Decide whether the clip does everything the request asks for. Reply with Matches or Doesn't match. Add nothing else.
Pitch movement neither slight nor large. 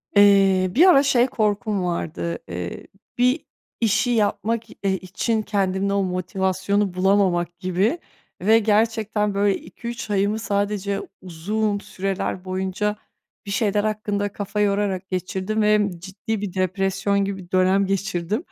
Doesn't match